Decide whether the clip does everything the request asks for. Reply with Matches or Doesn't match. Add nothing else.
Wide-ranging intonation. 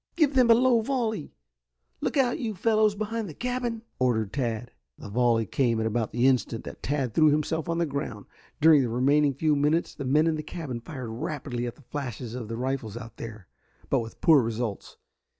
Matches